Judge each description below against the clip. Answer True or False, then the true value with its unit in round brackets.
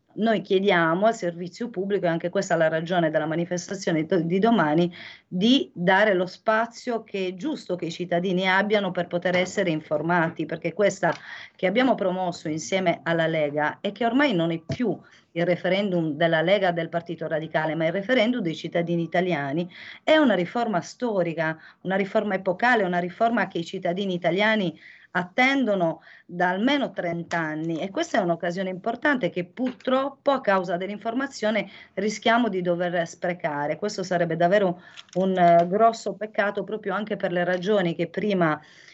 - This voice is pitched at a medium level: True (180 Hz)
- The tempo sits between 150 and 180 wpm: True (155 wpm)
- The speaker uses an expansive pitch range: False (3.6 semitones)